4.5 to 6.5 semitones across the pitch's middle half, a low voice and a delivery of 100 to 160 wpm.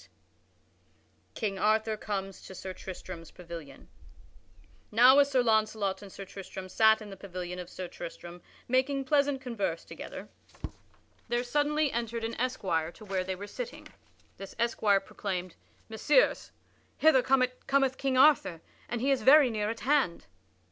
No: wide, 5.5 semitones; high, 220 Hz; average, 150 wpm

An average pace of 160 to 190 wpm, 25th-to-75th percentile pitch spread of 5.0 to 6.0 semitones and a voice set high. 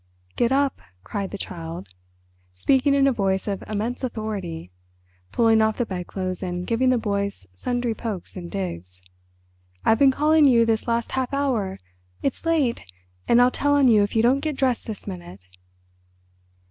Yes: average, 165 wpm; wide, 5.4 semitones; high, 225 Hz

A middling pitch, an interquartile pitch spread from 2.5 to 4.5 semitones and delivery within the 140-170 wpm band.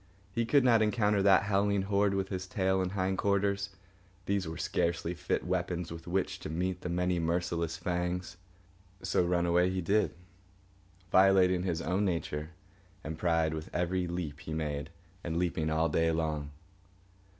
No: very low, 90 Hz; average, 2.8 semitones; average, 160 wpm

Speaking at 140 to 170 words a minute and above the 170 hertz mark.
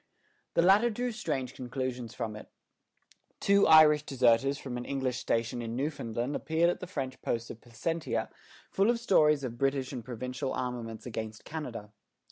No: average, 160 wpm; low, 130 Hz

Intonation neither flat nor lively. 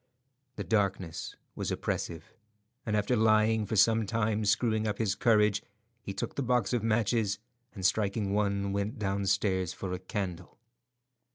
No: narrow, 2.0 semitones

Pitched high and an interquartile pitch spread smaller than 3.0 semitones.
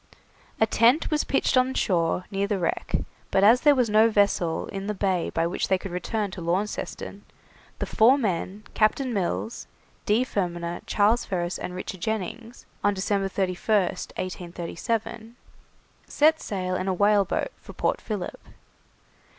No: high, 200 Hz; average, 3.4 semitones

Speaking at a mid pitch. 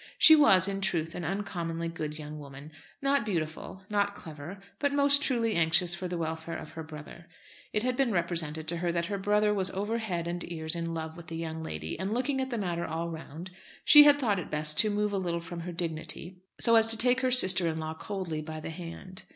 Yes: medium, 175 Hz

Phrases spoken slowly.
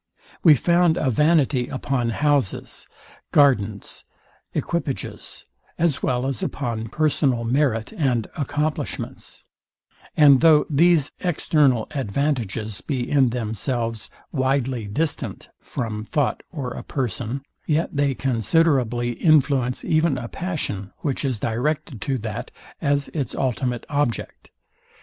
Yes: slow, 115 wpm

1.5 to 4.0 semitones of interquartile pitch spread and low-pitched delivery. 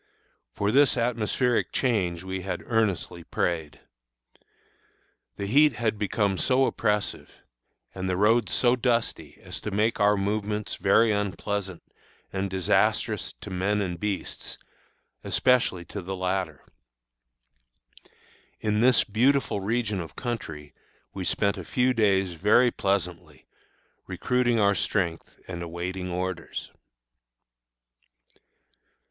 Yes: average, 3.7 semitones; low, 100 Hz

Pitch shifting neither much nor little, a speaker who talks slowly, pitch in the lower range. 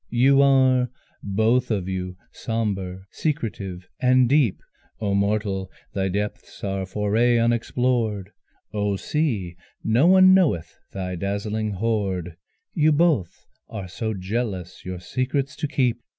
Yes: average, 4.9 semitones; slow, 120 wpm; low, 110 Hz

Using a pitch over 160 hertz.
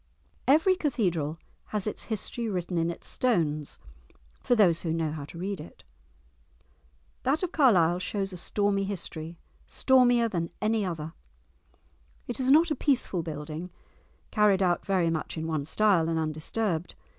Yes: medium, 185 Hz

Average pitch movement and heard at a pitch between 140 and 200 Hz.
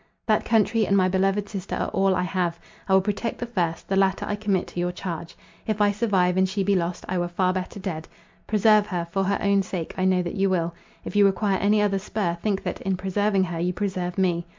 No: narrow, 2.1 semitones; high, 190 Hz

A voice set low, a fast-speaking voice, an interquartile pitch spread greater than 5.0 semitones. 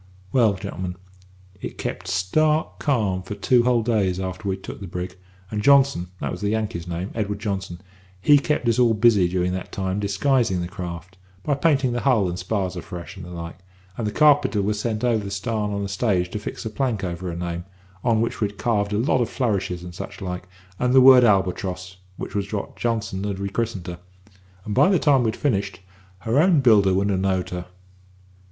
No: low, 100 Hz; fast, 210 wpm; average, 4.3 semitones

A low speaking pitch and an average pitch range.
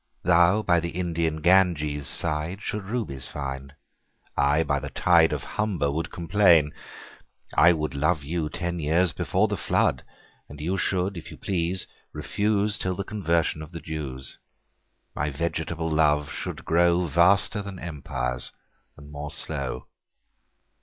Yes: very low, 80 Hz; average, 3.5 semitones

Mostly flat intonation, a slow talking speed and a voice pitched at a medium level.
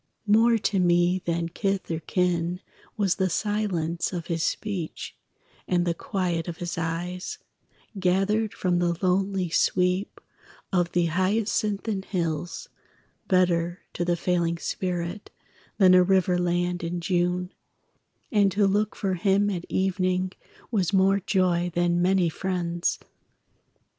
Yes: narrow, 2.0 semitones; slow, 130 wpm; medium, 180 Hz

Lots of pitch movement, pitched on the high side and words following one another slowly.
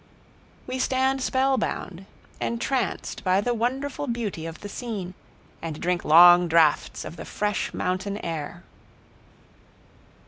Yes: wide, 6.3 semitones; high, 200 Hz; slow, 115 wpm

